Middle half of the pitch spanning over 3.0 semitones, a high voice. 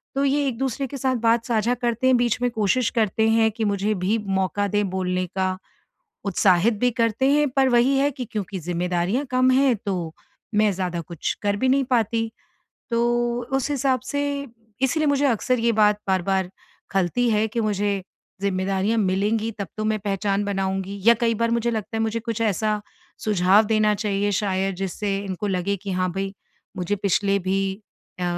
Yes: average, 3.5 semitones; high, 210 Hz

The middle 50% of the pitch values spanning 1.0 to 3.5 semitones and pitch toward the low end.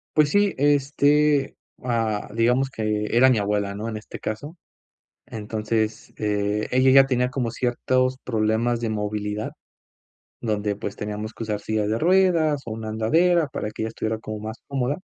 No: average, 4.0 semitones; low, 115 Hz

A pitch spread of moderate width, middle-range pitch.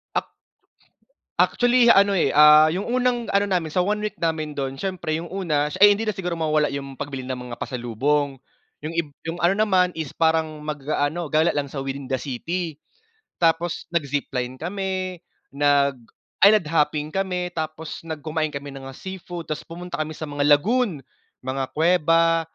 Yes: average, 4.0 semitones; medium, 160 Hz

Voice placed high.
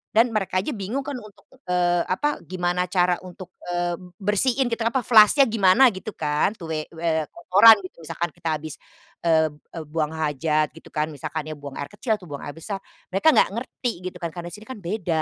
No: medium, 180 Hz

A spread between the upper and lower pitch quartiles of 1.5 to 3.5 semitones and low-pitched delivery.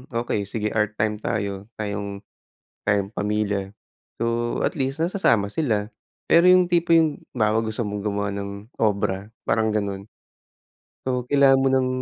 No: average, 4.0 semitones; low, 110 Hz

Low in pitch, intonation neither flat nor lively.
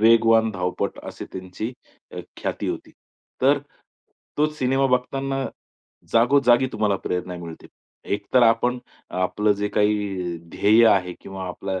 Yes: low, 110 Hz; average, 4.9 semitones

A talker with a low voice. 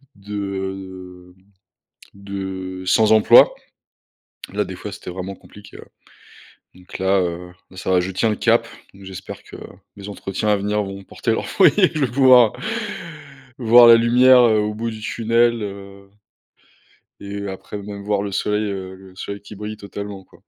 Yes: low, 100 Hz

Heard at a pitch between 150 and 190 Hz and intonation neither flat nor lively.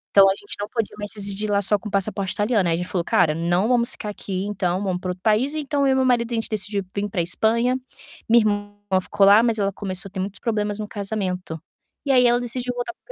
No: high, 205 Hz; average, 3.1 semitones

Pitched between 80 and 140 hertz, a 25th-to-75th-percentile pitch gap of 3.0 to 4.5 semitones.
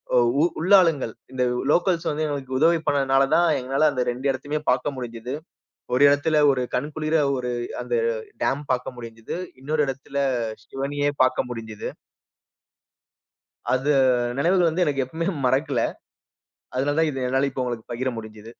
Yes: low, 135 Hz; average, 3.3 semitones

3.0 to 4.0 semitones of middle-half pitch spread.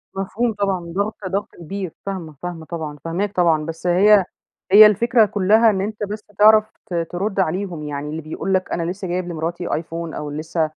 Yes: average, 3.6 semitones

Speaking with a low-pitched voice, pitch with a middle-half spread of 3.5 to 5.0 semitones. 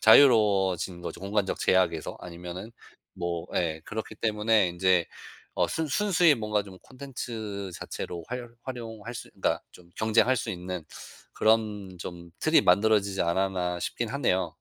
Yes: low, 100 Hz; average, 4.0 semitones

